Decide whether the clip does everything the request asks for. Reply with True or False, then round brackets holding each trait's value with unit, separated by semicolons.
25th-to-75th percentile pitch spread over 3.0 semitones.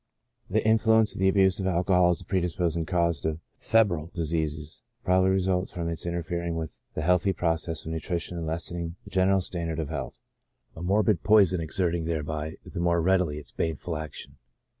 False (2.4 semitones)